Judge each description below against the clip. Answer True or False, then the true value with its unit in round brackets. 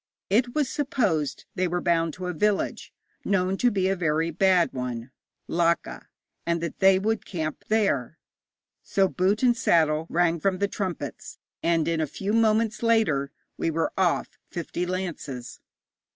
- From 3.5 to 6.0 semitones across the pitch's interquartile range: True (3.8 semitones)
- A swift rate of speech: False (155 wpm)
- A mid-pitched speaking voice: True (180 Hz)